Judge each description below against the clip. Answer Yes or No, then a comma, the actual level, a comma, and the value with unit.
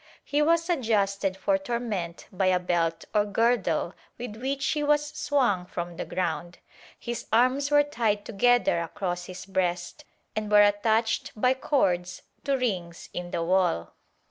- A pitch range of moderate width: No, wide, 6.0 semitones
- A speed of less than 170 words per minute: Yes, average, 150 wpm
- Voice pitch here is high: Yes, high, 210 Hz